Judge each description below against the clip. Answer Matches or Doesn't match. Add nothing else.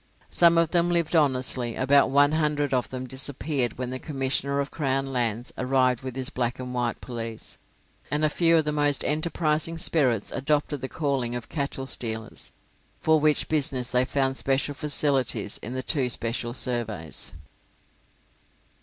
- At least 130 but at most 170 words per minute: Matches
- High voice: Doesn't match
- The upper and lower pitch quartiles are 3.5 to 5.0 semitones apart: Doesn't match